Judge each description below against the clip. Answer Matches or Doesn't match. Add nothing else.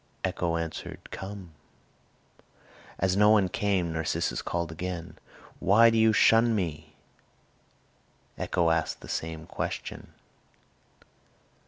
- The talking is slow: Matches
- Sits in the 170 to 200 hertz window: Doesn't match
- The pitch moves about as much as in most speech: Matches